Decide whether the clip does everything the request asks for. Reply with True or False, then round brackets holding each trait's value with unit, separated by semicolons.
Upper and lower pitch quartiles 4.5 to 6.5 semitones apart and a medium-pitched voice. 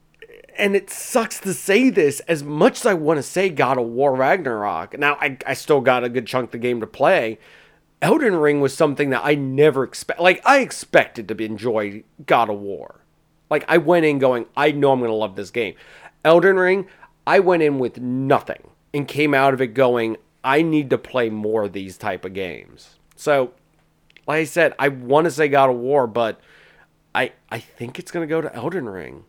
True (4.9 semitones; 145 Hz)